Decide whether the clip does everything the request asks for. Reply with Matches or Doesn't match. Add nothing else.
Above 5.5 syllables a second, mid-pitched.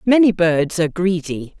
Doesn't match